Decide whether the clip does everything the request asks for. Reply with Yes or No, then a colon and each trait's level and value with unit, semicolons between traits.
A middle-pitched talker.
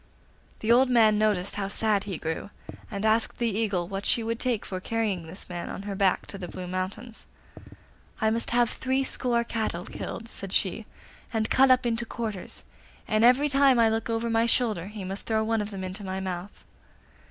No: high, 220 Hz